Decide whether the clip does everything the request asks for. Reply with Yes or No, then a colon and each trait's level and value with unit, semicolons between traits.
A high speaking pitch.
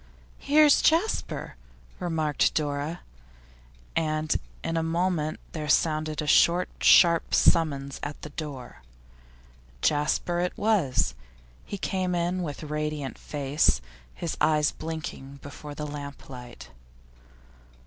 No: medium, 155 Hz